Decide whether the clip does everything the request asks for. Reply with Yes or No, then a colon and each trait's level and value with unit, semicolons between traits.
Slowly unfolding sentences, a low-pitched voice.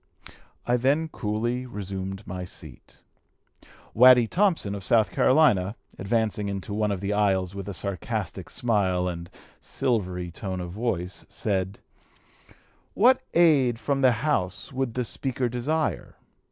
Yes: slow, 130 wpm; low, 105 Hz